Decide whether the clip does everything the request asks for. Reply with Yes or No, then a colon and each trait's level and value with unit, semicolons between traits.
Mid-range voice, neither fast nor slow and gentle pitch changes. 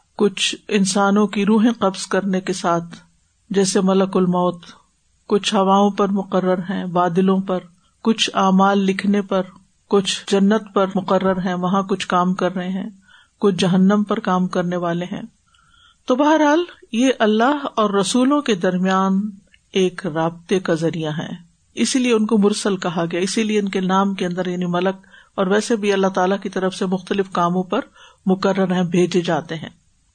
No: high, 195 Hz; average, 170 wpm; narrow, 2.1 semitones